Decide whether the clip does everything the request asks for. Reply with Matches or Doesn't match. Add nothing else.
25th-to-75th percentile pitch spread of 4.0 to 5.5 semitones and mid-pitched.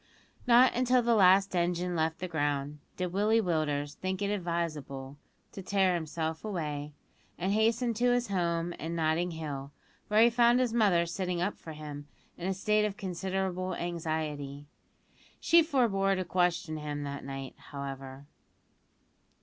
Matches